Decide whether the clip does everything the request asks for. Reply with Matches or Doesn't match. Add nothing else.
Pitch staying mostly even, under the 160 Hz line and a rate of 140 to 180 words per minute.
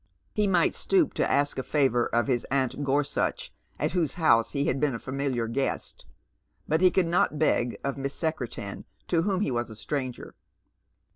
Doesn't match